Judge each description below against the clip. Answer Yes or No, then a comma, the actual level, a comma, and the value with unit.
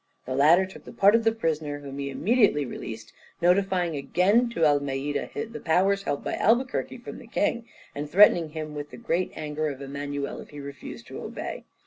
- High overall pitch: No, medium, 160 Hz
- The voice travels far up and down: Yes, wide, 5.7 semitones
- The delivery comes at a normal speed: Yes, average, 190 wpm